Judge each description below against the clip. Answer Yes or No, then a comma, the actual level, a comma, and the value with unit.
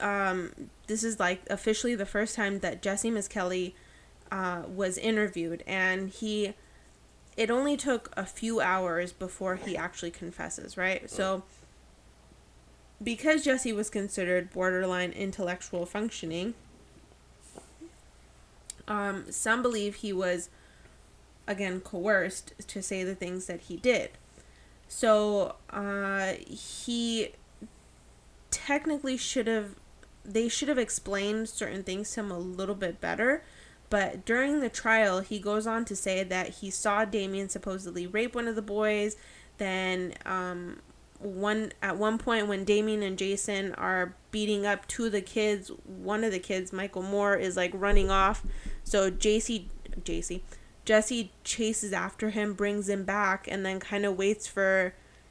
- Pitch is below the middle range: No, high, 200 Hz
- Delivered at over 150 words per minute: No, average, 140 wpm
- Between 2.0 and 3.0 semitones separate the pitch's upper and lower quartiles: Yes, average, 2.7 semitones